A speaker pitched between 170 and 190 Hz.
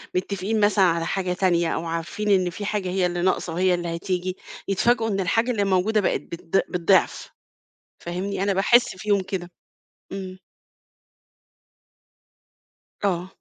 Yes: medium, 185 Hz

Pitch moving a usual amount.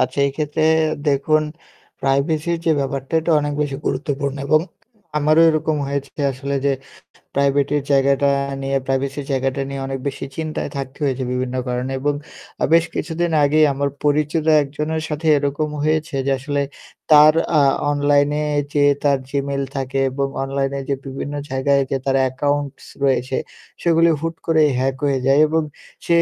No: narrow, 1.9 semitones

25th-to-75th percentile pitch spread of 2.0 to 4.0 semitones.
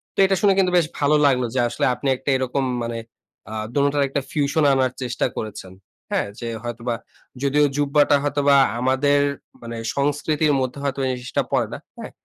Yes: narrow, 2.5 semitones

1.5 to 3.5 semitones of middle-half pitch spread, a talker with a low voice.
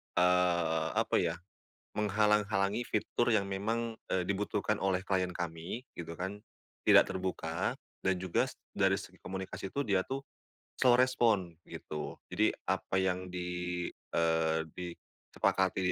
Yes: average, 2.8 semitones; very low, 95 Hz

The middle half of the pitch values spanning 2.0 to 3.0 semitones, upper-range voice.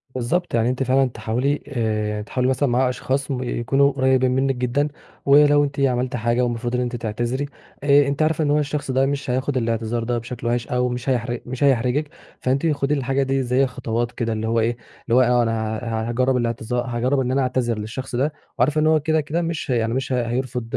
No: narrow, 2.6 semitones; low, 125 Hz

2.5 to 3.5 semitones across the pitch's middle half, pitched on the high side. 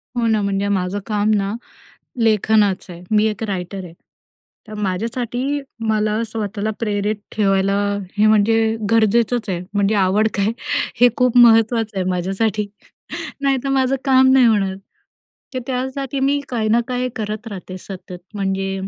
Yes: average, 3.2 semitones; high, 215 Hz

